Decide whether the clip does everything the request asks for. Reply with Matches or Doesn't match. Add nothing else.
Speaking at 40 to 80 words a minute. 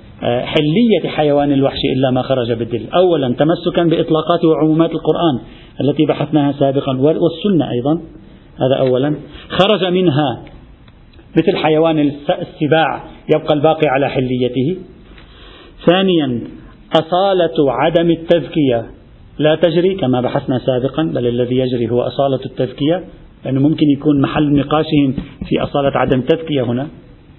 Doesn't match